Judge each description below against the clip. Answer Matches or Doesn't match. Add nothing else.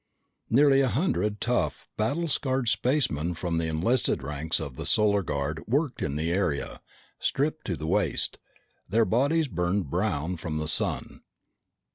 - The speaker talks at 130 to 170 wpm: Matches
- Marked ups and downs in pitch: Matches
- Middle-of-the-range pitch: Doesn't match